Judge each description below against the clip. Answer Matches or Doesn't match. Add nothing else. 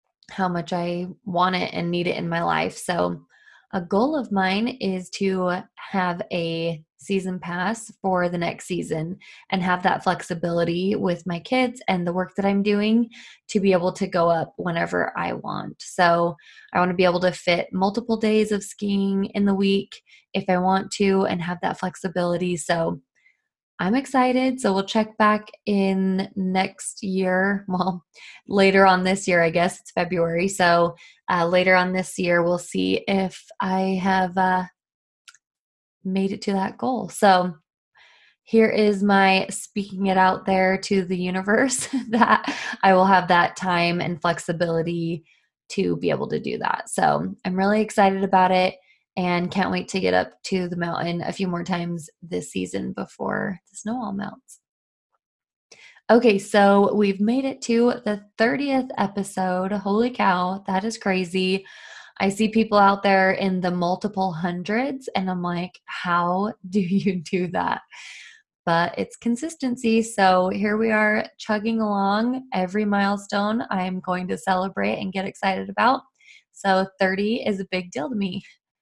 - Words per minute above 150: Matches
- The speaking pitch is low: Doesn't match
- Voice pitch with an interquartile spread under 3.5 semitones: Matches